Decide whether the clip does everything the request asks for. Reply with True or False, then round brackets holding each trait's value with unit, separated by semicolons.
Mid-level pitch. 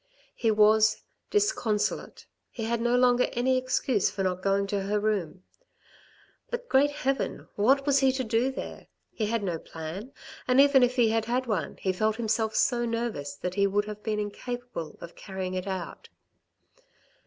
False (220 Hz)